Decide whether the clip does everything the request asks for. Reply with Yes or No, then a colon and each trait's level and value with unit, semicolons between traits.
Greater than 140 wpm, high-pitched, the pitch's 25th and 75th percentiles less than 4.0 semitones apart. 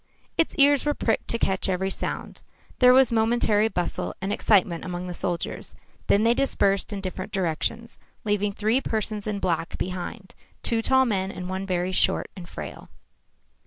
Yes: average, 165 wpm; high, 200 Hz; average, 3.6 semitones